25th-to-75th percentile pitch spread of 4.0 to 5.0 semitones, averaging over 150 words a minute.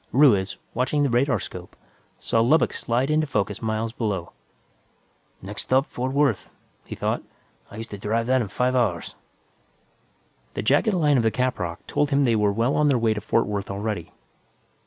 Yes: average, 4.3 semitones; average, 175 wpm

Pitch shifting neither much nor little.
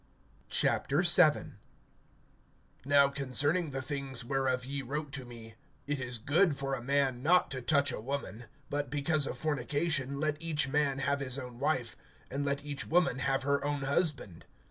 No: narrow, 1.8 semitones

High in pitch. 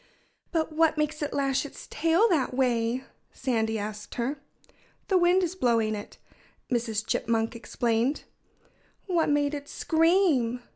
Yes: very high, 270 Hz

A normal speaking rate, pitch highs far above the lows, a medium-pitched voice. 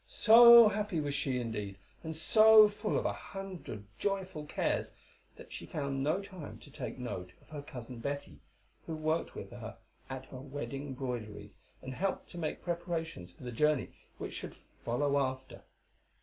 Yes: average, 165 wpm; wide, 5.7 semitones; medium, 145 Hz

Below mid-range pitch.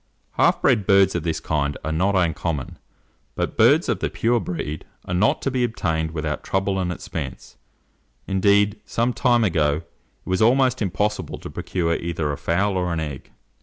Yes: very low, 90 Hz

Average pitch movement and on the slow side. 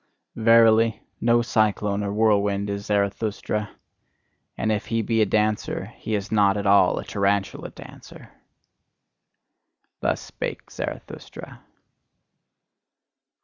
No: narrow, 1.6 semitones; slow, 105 wpm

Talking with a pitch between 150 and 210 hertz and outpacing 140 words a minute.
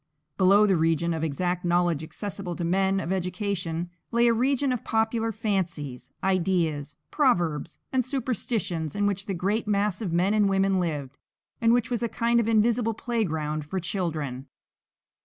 Yes: high, 190 Hz; average, 160 wpm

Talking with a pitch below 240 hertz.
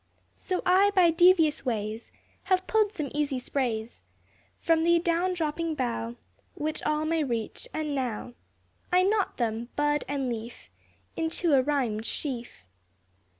No: very high, 295 Hz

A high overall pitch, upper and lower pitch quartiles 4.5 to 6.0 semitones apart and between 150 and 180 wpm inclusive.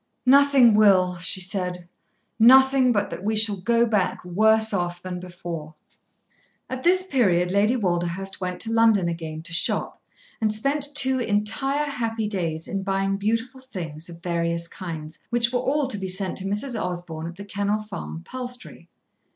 Yes: high, 200 Hz; average, 5.0 semitones; average, 165 wpm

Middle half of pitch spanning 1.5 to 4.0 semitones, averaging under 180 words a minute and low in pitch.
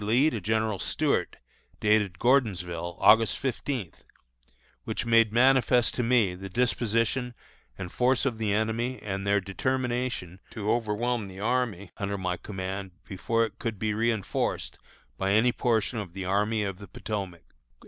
Yes: average, 3.6 semitones; average, 150 wpm; low, 110 Hz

